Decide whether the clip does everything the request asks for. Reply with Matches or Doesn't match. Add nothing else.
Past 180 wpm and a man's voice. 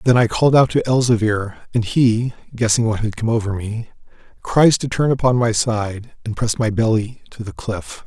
Matches